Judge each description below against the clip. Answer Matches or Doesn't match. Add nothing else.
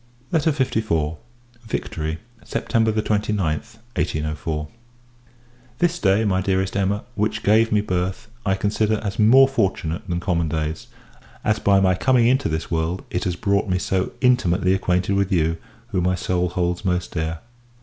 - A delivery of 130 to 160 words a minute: Matches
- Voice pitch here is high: Doesn't match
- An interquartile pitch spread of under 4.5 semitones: Matches